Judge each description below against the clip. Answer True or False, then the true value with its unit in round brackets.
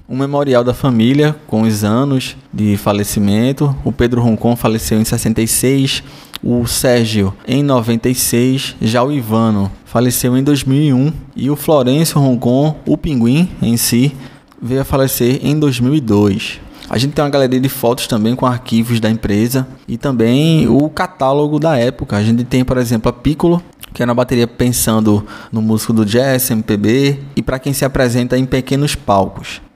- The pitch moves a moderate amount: True (3.2 semitones)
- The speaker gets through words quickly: False (165 wpm)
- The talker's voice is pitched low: True (125 Hz)